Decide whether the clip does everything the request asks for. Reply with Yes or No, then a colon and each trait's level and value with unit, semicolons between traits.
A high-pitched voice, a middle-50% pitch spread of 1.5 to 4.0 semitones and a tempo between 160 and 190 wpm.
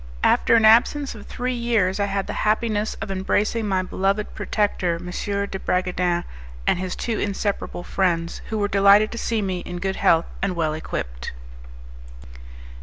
Yes: high, 195 Hz; average, 3.0 semitones; average, 165 wpm